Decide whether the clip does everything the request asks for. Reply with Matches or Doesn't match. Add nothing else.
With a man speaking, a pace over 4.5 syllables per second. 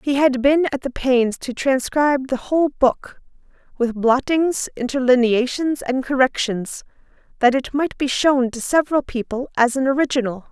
Doesn't match